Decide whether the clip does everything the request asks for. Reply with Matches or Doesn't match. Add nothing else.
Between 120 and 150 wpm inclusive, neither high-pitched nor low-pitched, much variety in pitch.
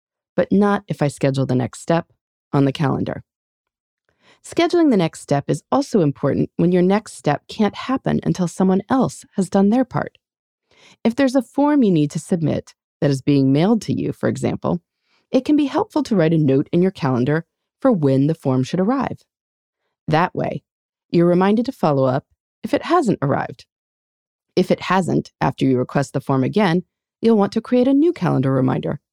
Doesn't match